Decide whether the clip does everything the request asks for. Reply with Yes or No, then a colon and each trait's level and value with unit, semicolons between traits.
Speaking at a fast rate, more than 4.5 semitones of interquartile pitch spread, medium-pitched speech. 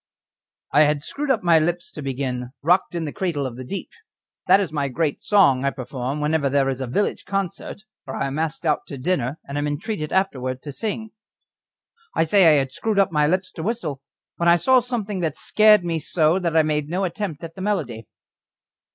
Yes: fast, 210 wpm; average, 5.3 semitones; medium, 160 Hz